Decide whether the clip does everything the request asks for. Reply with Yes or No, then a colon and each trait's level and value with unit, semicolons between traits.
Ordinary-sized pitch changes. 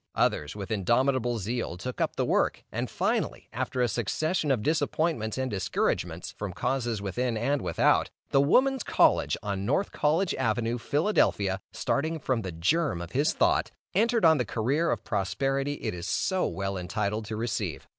No: wide, 6.1 semitones